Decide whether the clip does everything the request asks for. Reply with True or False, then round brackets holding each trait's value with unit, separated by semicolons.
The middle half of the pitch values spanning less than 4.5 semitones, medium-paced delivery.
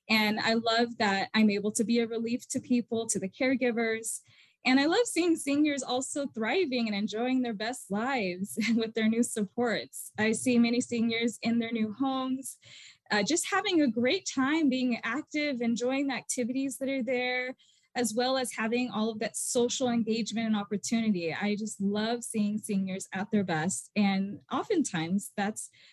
True (3.2 semitones; 175 wpm)